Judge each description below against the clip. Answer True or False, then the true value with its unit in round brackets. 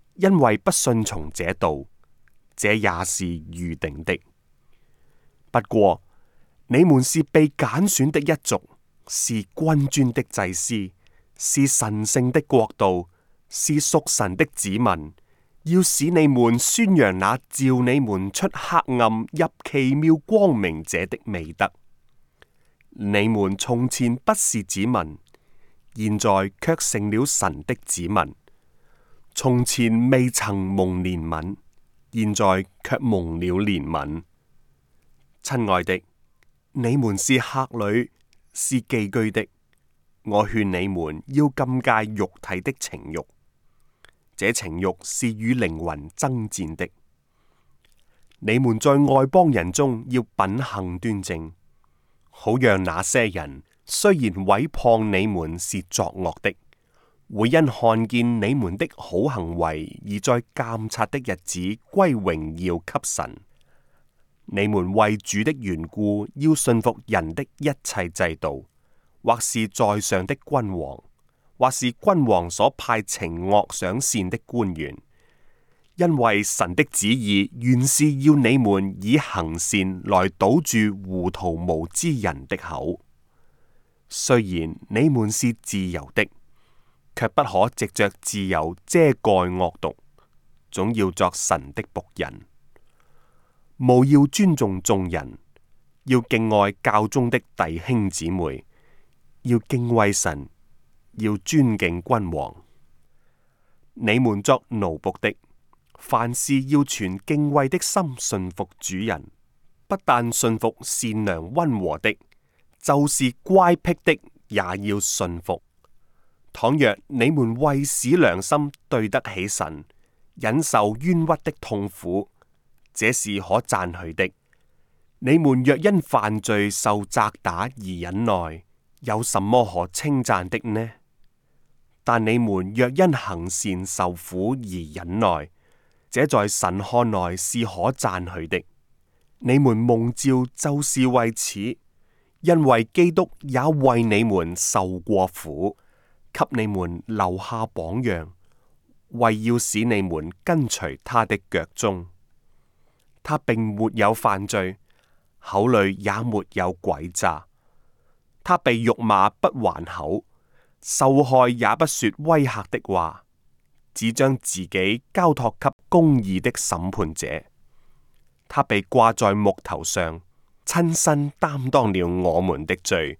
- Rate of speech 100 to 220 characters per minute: True (170 characters per minute)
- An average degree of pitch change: False (5.8 semitones)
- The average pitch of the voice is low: True (105 Hz)